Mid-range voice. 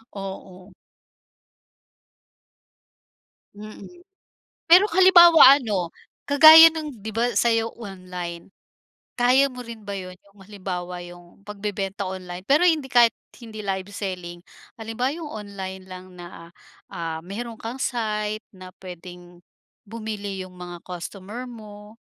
No: high, 205 Hz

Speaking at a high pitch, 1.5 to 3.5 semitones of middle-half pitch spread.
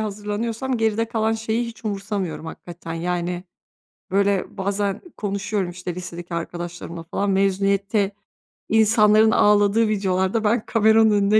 Yes: high, 200 Hz; average, 2.9 semitones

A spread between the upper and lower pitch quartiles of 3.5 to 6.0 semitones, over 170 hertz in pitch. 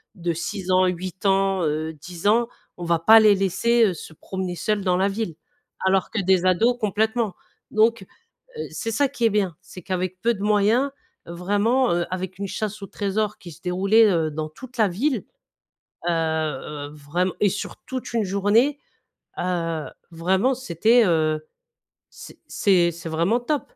Yes: average, 4.1 semitones; high, 190 Hz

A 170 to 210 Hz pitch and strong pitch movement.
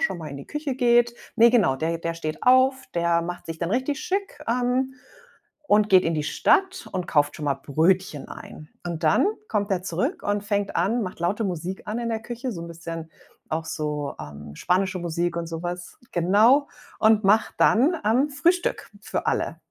Yes: medium, 185 Hz; wide, 6.2 semitones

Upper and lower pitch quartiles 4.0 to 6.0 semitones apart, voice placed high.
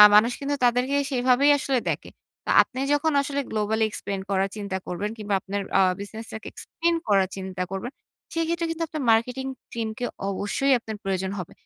Yes: wide, 5.5 semitones; high, 225 Hz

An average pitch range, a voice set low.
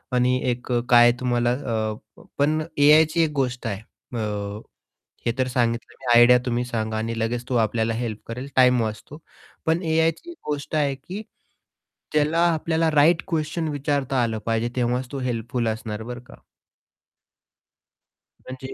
Yes: average, 4.1 semitones; low, 125 Hz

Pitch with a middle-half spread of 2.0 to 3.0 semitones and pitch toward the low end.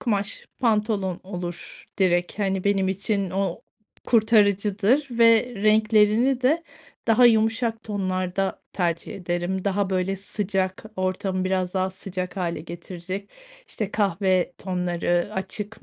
No: narrow, 2.5 semitones; high, 195 Hz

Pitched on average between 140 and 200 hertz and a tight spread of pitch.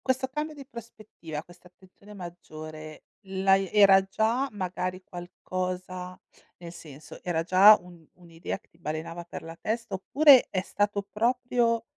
No: medium, 185 Hz; average, 4.0 semitones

